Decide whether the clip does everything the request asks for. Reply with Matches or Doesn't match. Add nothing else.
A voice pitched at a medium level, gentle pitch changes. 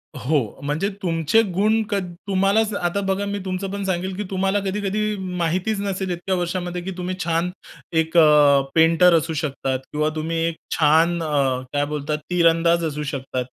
Doesn't match